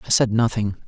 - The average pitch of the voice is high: No, low, 110 Hz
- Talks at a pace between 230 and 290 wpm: No, fast, 205 wpm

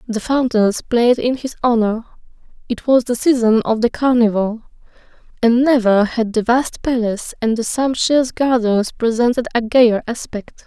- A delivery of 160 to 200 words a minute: No, average, 150 wpm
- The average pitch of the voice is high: Yes, high, 235 Hz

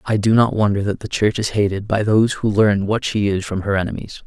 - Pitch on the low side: Yes, low, 105 Hz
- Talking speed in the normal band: No, fast, 265 wpm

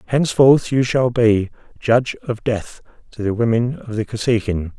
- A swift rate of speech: No, average, 165 wpm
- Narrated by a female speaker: No, male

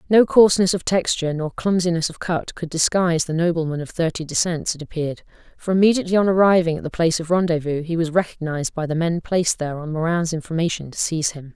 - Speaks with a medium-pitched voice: Yes, medium, 165 Hz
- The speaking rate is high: Yes, fast, 210 wpm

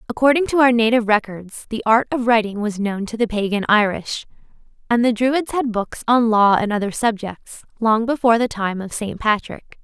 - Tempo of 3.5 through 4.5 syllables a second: No, 5.3 syllables/s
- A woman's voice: Yes, female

